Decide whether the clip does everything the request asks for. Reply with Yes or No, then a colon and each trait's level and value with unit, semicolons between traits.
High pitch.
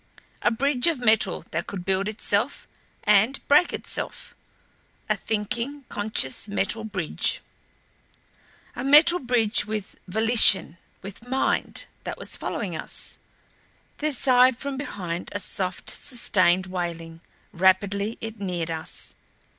Yes: high, 210 Hz